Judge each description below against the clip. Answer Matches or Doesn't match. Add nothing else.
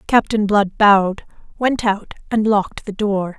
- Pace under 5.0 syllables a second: Matches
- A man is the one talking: Doesn't match